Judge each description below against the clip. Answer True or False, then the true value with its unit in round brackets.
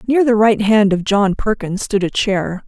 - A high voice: True (205 Hz)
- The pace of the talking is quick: True (225 wpm)